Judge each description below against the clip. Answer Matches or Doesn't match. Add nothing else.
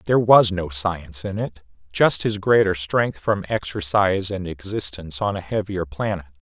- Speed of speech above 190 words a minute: Doesn't match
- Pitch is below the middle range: Matches